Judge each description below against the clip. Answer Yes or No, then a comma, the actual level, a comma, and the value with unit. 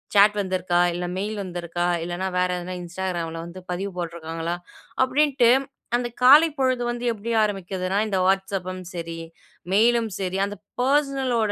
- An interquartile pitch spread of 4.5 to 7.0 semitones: Yes, average, 5.1 semitones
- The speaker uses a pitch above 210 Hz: No, high, 190 Hz